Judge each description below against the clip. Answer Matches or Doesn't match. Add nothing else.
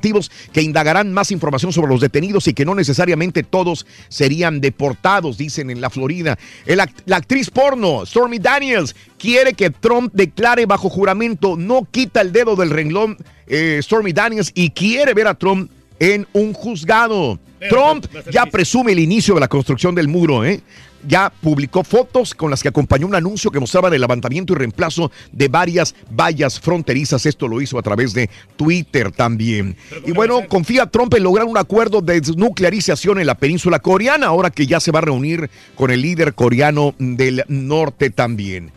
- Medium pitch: Matches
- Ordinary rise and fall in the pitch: Doesn't match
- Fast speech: Doesn't match